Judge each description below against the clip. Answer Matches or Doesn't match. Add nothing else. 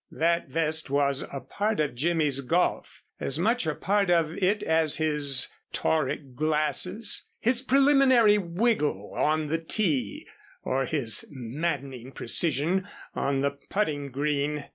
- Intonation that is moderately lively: Matches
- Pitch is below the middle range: Doesn't match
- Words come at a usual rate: Doesn't match